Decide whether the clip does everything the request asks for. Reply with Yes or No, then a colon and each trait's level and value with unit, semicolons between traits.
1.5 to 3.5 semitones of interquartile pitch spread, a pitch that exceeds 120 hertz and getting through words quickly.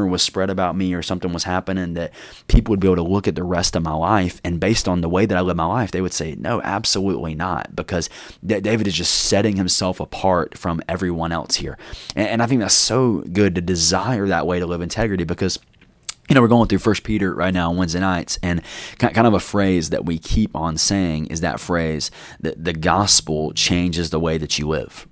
No: average, 2.8 semitones; very low, 90 Hz; fast, 230 wpm